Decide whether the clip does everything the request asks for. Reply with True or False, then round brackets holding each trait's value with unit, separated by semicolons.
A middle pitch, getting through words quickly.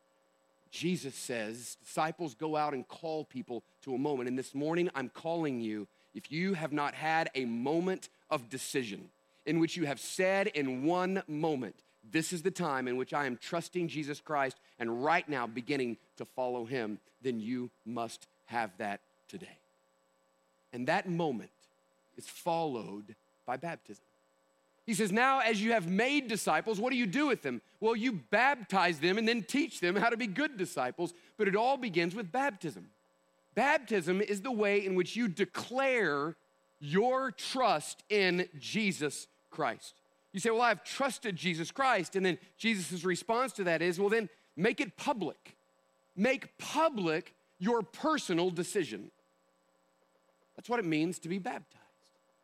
False (165 Hz; 165 wpm)